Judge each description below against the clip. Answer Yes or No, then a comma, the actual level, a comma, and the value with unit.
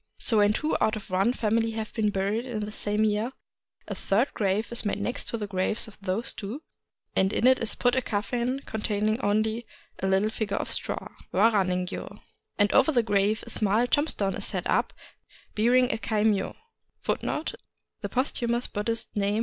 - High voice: Yes, high, 215 Hz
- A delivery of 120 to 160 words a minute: No, average, 175 wpm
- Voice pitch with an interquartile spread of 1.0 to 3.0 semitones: Yes, narrow, 2.4 semitones